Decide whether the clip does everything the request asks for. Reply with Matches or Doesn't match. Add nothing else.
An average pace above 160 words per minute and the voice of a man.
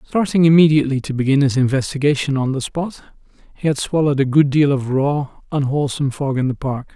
Matches